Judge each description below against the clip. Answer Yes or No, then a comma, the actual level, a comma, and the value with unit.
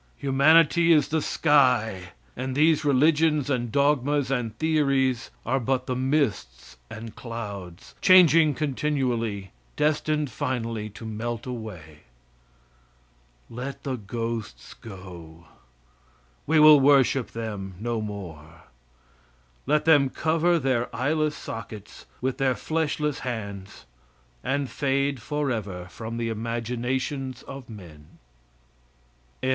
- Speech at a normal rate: No, slow, 105 wpm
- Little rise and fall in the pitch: No, average, 4.8 semitones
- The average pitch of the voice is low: Yes, low, 125 Hz